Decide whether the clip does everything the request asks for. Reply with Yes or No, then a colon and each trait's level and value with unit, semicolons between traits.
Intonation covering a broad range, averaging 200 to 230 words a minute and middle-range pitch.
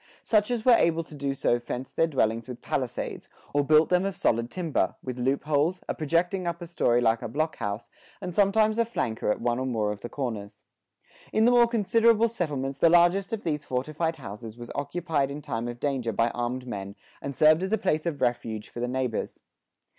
Yes: wide, 6.6 semitones; fast, 205 wpm; medium, 145 Hz